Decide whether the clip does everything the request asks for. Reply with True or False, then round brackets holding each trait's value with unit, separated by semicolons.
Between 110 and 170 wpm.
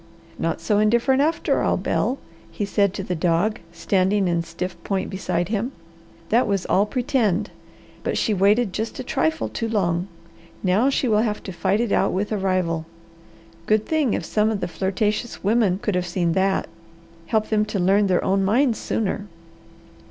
False (180 wpm)